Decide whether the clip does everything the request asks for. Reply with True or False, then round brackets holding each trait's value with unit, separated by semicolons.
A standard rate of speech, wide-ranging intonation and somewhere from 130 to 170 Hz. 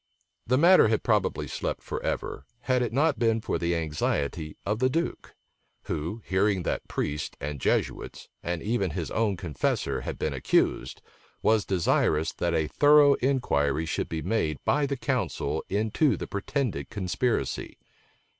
False (150 wpm; 7.5 semitones; 100 Hz)